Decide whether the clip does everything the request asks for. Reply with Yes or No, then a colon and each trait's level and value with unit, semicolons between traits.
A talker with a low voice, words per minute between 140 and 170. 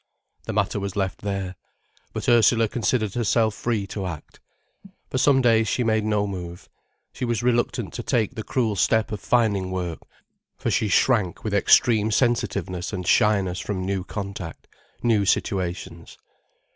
Yes: low, 105 Hz; average, 155 wpm